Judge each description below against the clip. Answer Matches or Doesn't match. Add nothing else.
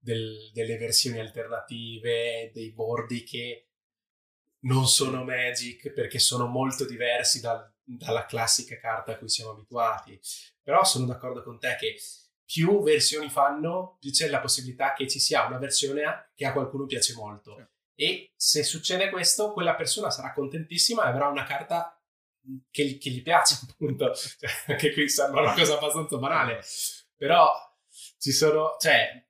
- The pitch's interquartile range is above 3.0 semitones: Matches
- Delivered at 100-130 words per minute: Doesn't match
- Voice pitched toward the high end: Doesn't match